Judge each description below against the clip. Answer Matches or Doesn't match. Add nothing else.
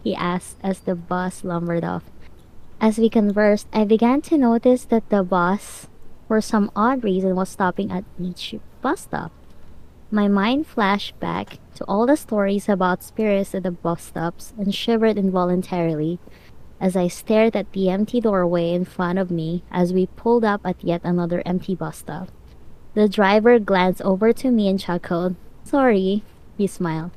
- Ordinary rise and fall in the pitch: Matches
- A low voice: Doesn't match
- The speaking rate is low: Doesn't match